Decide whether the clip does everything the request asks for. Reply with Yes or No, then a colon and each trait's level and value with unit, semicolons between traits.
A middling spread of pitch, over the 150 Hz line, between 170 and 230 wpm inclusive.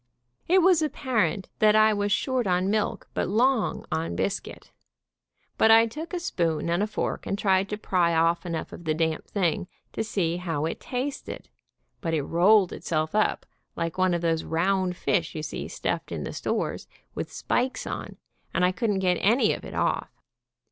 Yes: average, 4.5 semitones; high, 190 Hz; average, 190 wpm